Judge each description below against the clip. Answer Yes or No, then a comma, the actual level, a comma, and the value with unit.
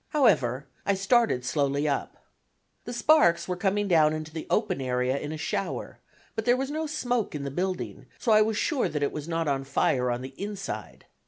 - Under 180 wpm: No, average, 200 wpm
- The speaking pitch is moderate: Yes, medium, 170 Hz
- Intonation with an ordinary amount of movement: No, wide, 7.5 semitones